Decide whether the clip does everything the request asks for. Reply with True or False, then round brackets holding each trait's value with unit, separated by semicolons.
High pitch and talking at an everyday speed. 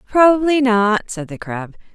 True (230 Hz; 155 wpm)